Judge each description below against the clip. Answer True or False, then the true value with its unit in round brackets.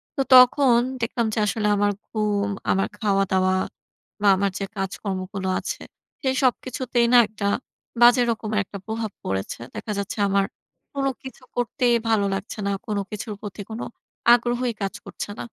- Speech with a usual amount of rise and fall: True (3.3 semitones)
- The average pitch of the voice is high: True (215 Hz)